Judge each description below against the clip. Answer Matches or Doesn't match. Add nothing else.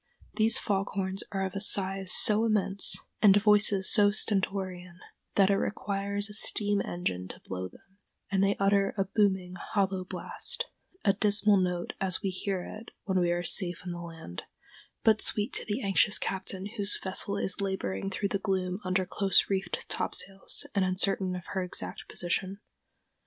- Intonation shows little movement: Matches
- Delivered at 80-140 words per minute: Doesn't match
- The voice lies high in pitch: Matches